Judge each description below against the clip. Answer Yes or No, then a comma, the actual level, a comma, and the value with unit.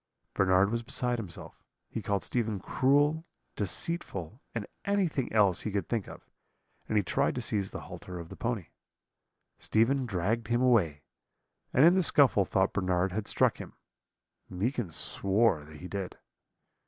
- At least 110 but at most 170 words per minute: Yes, average, 155 wpm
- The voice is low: Yes, low, 105 Hz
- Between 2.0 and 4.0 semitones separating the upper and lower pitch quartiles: No, average, 4.8 semitones